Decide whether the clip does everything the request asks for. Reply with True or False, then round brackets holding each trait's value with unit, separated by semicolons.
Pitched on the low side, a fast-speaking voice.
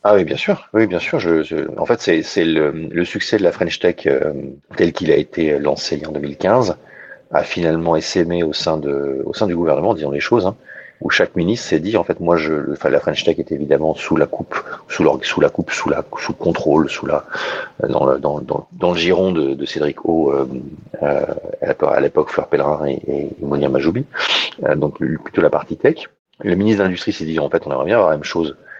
True (85 Hz; 235 wpm)